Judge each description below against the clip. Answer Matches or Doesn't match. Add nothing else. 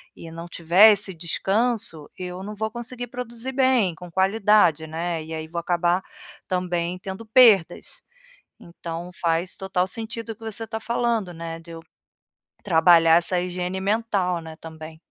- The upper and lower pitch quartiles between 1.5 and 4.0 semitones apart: Doesn't match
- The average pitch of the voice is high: Doesn't match